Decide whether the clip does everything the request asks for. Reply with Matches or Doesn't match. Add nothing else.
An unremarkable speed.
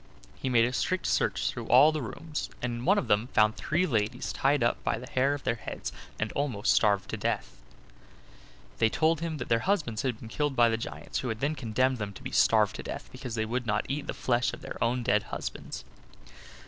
Doesn't match